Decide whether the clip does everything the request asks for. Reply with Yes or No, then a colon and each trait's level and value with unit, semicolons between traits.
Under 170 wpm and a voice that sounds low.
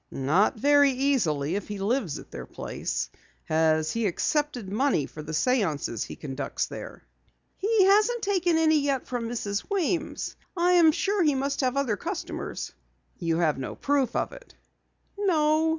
No: average, 160 wpm; very high, 265 Hz